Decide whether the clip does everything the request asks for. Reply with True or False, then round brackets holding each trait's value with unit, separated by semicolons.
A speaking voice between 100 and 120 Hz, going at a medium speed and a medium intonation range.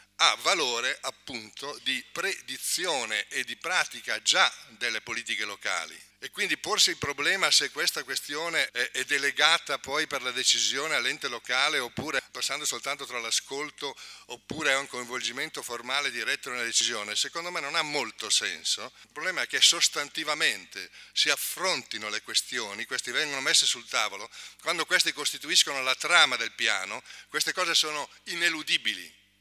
False (140 Hz; 145 wpm; 4.4 semitones)